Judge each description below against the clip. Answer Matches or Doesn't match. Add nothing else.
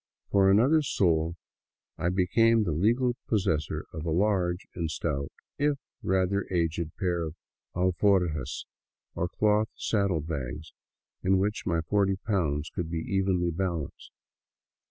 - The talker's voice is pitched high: Doesn't match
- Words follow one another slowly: Matches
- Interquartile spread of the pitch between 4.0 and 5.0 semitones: Doesn't match